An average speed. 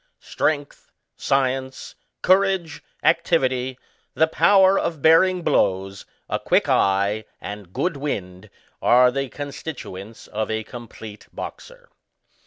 No: slow, 110 wpm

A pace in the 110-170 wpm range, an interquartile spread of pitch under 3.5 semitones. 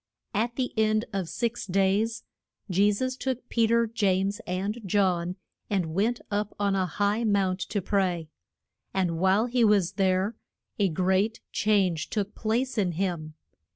Yes: average, 155 wpm; average, 2.9 semitones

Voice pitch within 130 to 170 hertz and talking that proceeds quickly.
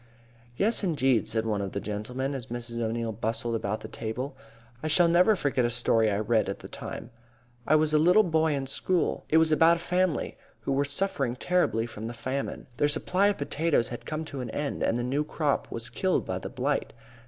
Yes: low, 135 Hz; fast, 215 wpm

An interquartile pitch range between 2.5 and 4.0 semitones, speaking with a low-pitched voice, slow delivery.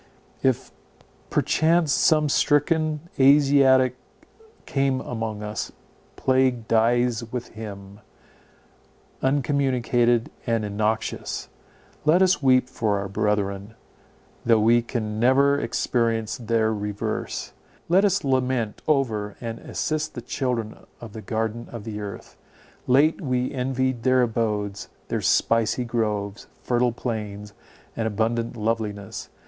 Yes: average, 3.3 semitones; low, 120 Hz; slow, 110 wpm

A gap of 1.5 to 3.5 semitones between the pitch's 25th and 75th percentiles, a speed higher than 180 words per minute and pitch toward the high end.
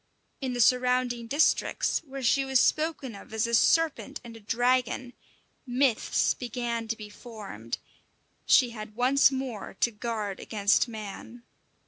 No: average, 2.7 semitones; average, 140 wpm; high, 240 Hz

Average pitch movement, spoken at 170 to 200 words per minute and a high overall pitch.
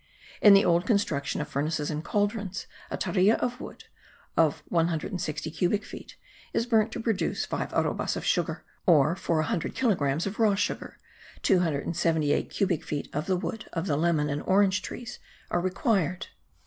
No: average, 4.7 semitones; average, 175 wpm; medium, 175 Hz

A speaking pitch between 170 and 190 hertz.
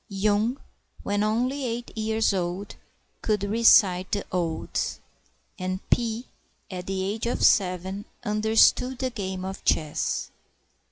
No: high, 205 Hz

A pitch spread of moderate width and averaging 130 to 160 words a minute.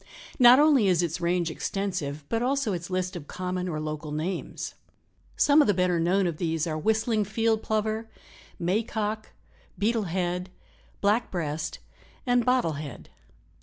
Yes: average, 4.7 semitones; average, 155 wpm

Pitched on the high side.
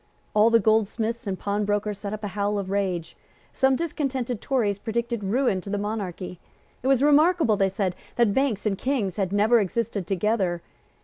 Yes: high, 210 Hz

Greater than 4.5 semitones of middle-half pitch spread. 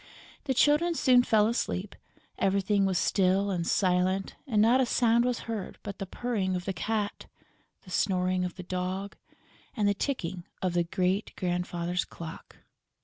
No: average, 3.4 semitones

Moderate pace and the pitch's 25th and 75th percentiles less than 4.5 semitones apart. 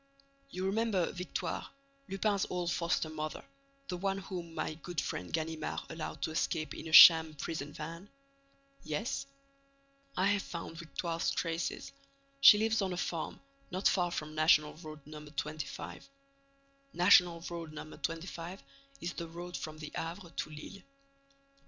Yes: average, 145 wpm; average, 2.7 semitones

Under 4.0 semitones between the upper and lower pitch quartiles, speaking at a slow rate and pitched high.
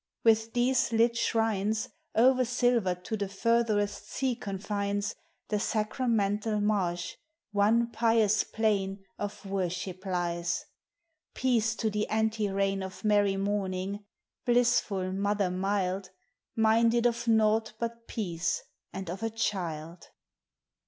Yes: average, 2.7 semitones; slow, 115 wpm; high, 210 Hz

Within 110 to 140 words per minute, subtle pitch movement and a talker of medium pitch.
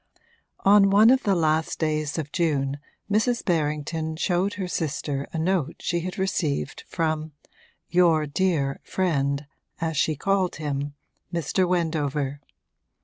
No: slow, 135 wpm; average, 3.7 semitones; medium, 160 Hz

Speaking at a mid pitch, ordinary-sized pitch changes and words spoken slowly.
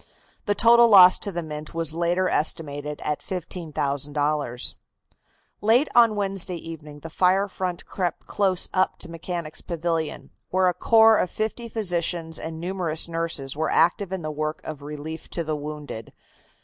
No: medium, 170 Hz; average, 3.5 semitones; average, 155 wpm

